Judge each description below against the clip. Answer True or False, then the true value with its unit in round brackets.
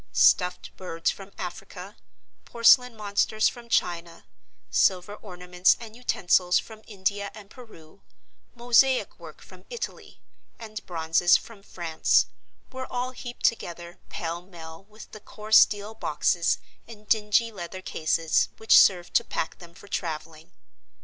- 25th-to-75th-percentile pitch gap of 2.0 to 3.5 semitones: False (4.2 semitones)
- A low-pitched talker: False (200 Hz)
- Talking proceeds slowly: True (130 wpm)